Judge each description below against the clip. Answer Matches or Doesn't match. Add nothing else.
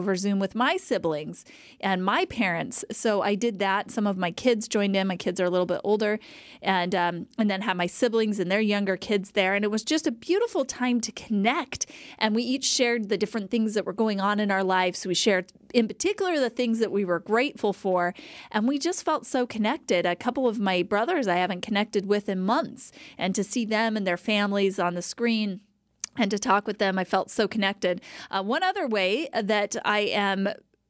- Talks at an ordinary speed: Doesn't match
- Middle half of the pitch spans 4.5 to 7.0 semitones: Doesn't match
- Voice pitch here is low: Doesn't match